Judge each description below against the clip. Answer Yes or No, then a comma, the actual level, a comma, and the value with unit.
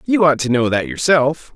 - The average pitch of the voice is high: No, medium, 140 Hz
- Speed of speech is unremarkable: No, fast, 230 wpm